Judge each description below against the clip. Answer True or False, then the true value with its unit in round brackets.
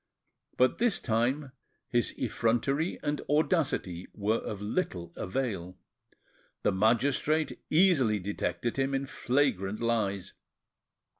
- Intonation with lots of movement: True (5.8 semitones)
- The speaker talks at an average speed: False (100 wpm)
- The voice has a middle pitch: False (120 Hz)